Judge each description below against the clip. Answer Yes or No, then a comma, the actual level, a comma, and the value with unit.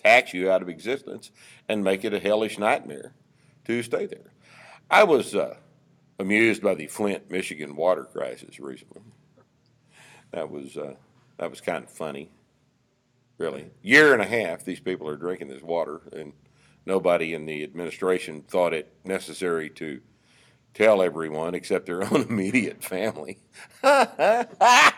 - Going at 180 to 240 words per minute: No, average, 145 wpm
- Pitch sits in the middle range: No, very low, 95 Hz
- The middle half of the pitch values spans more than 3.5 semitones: Yes, average, 5.0 semitones